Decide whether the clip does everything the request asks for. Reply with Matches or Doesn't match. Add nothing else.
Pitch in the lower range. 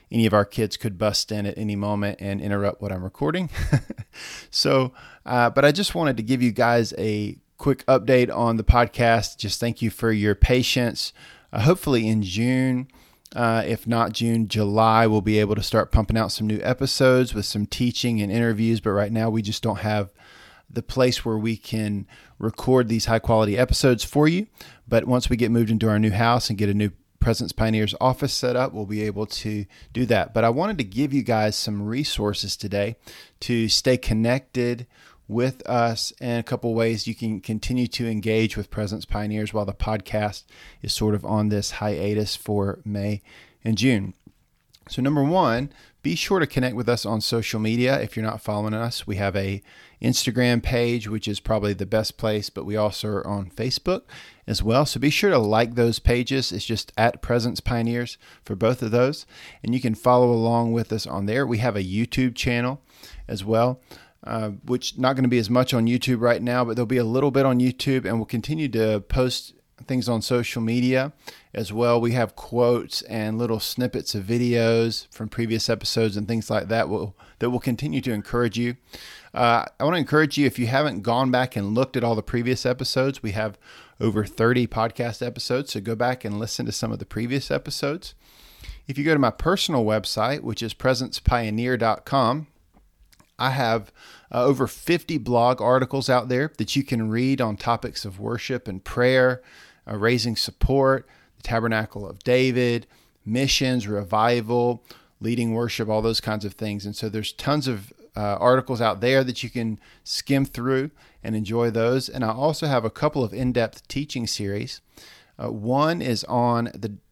Matches